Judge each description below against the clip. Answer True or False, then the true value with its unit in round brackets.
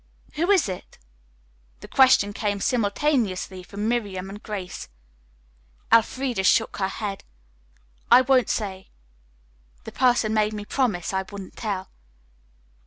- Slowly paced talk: True (120 wpm)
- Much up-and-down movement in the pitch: False (4.0 semitones)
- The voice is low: False (210 Hz)